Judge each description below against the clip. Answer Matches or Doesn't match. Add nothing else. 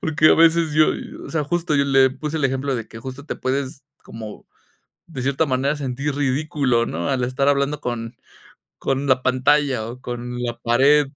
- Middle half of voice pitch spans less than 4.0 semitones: Matches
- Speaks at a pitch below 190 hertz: Matches